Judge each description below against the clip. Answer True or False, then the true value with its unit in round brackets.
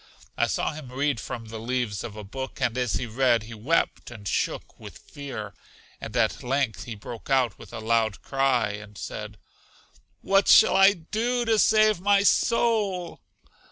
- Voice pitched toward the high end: False (130 Hz)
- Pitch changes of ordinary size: False (8.2 semitones)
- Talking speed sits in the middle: True (175 wpm)